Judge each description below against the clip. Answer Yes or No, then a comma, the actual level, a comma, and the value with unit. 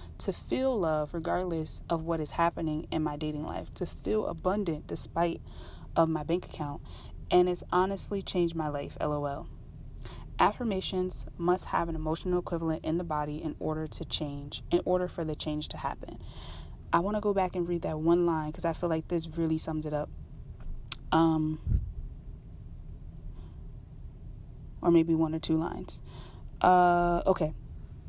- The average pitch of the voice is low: No, medium, 160 Hz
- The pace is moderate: Yes, average, 160 wpm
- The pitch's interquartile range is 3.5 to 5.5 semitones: No, narrow, 2.4 semitones